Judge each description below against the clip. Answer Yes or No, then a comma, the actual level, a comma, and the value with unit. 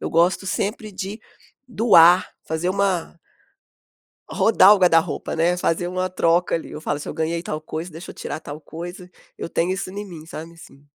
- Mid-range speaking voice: Yes, medium, 175 Hz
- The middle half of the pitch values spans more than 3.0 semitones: No, narrow, 2.4 semitones